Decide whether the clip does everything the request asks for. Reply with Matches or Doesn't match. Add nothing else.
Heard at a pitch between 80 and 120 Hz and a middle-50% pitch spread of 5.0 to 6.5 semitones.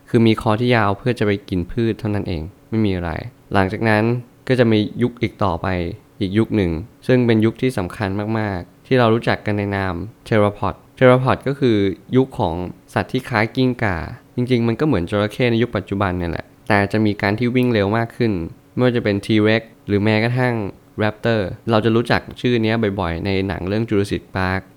Doesn't match